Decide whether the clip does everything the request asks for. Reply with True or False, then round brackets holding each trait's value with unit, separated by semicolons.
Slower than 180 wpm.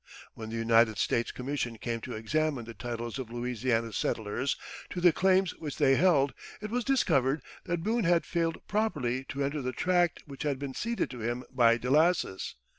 False (185 wpm)